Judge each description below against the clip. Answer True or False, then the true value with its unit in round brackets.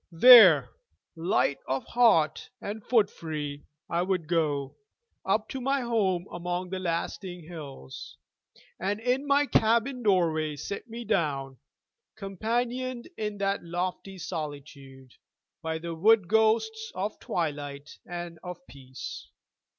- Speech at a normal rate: False (120 wpm)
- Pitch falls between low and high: True (180 Hz)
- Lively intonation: True (6.0 semitones)